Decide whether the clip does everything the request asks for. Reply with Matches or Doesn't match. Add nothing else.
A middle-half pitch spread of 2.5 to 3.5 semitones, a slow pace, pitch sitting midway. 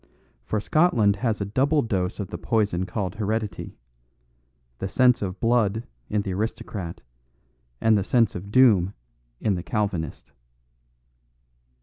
Doesn't match